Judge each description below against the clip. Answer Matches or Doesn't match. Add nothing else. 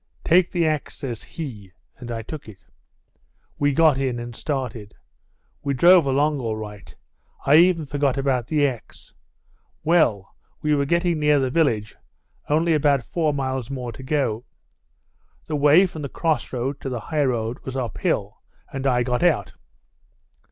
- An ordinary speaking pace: Matches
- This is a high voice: Doesn't match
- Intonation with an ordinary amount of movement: Matches